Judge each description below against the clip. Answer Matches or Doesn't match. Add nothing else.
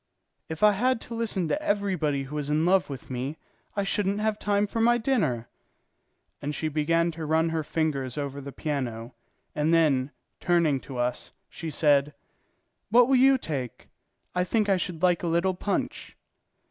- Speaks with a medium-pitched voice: Matches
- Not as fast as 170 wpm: Doesn't match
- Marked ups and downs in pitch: Matches